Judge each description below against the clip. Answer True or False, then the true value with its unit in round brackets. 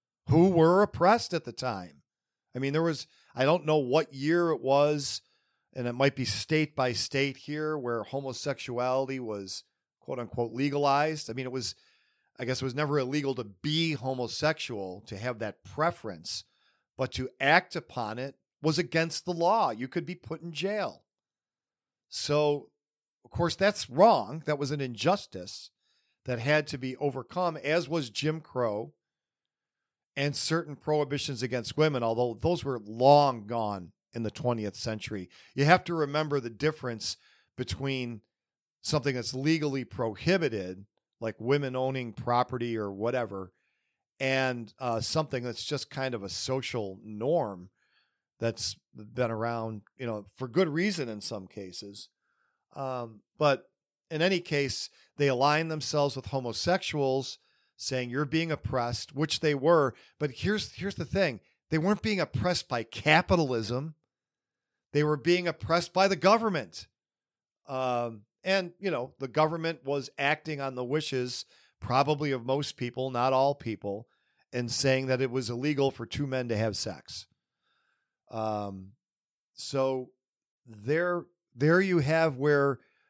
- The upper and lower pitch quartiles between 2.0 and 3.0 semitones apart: False (4.5 semitones)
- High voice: False (135 Hz)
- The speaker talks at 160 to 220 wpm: False (150 wpm)